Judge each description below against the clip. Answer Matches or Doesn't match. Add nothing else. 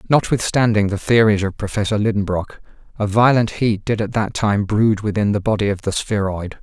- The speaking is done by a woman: Doesn't match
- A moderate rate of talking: Matches